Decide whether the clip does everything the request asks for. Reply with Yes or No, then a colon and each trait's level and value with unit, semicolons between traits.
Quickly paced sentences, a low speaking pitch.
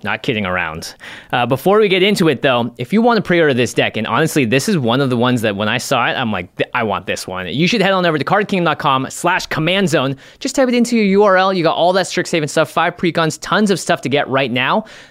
No: fast, 270 wpm; medium, 160 Hz